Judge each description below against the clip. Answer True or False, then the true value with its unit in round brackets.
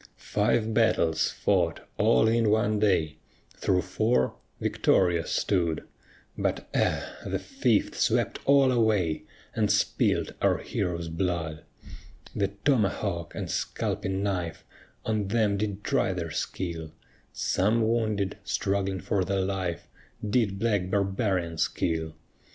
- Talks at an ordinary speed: False (115 wpm)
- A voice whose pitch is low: True (95 Hz)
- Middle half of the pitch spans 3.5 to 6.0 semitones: True (3.8 semitones)